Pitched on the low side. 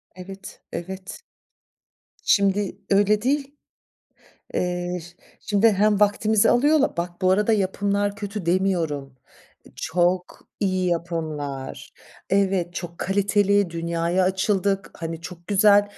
No: high, 190 Hz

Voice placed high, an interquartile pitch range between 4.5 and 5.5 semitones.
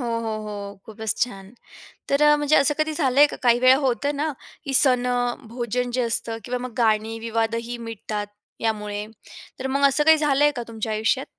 No: high, 245 Hz; average, 3.7 semitones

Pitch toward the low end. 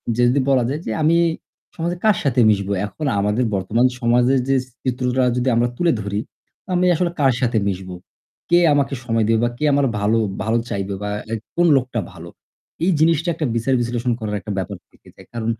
Yes: low, 120 Hz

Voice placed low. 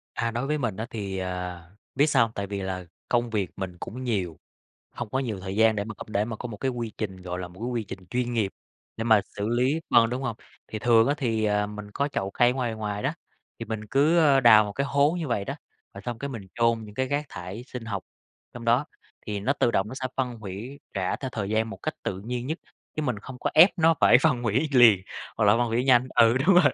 Yes: low, 115 Hz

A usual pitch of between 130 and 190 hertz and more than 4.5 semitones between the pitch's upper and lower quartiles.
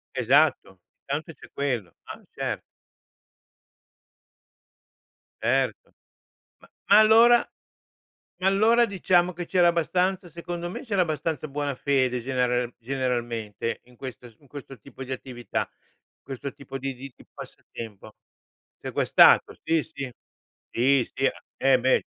Yes: medium, 140 Hz; wide, 5.6 semitones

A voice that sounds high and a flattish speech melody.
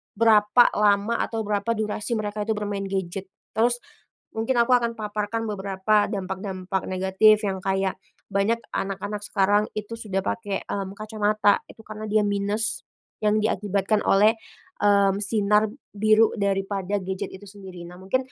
Yes: high, 205 Hz; narrow, 1.7 semitones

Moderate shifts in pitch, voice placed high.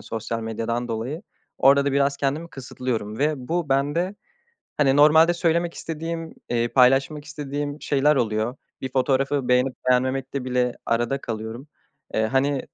No: average, 3.0 semitones; low, 135 Hz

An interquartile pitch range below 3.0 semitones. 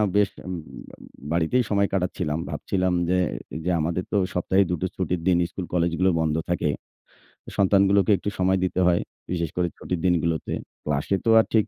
Yes: narrow, 2.4 semitones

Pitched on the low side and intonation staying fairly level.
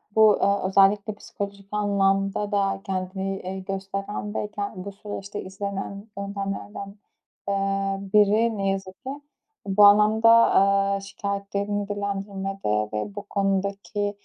No: high, 200 Hz; narrow, 0.8 semitones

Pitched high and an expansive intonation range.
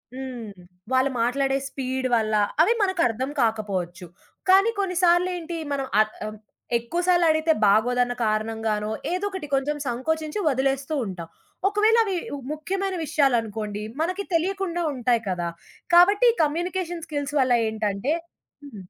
Yes: very high, 275 Hz; wide, 7.7 semitones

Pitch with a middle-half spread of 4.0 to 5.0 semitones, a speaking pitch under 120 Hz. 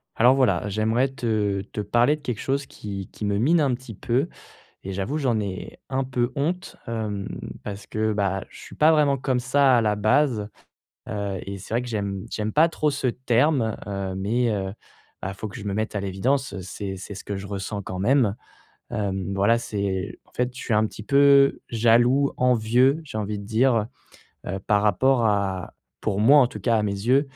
Yes: average, 4.5 semitones; low, 110 Hz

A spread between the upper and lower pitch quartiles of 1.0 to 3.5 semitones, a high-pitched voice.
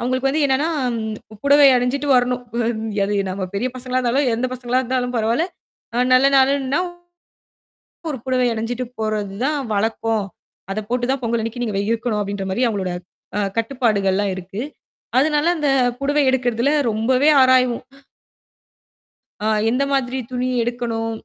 Yes: average, 2.9 semitones; high, 245 Hz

